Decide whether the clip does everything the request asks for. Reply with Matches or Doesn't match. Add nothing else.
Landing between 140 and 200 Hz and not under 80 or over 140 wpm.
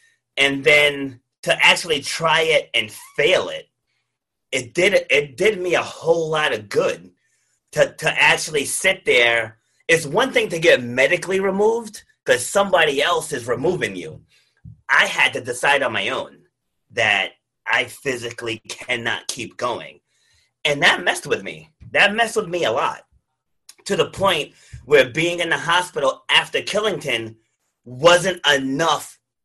Doesn't match